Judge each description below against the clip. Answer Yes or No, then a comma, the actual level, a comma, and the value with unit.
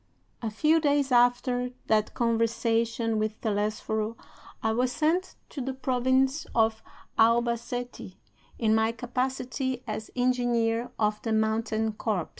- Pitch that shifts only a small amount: Yes, narrow, 2.3 semitones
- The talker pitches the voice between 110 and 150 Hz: No, high, 235 Hz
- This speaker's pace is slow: Yes, slow, 125 wpm